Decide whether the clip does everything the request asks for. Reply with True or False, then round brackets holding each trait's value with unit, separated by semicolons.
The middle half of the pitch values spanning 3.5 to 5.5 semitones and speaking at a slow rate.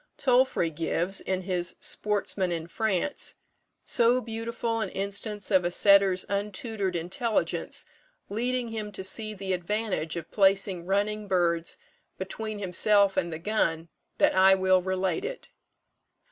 False (3.0 semitones; 130 wpm)